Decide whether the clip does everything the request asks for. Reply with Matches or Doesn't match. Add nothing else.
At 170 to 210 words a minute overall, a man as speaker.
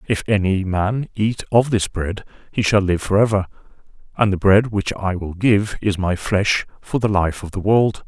Matches